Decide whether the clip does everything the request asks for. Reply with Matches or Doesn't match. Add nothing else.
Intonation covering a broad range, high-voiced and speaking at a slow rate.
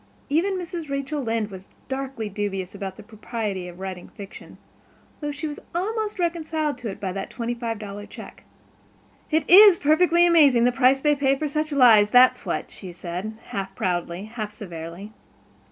Doesn't match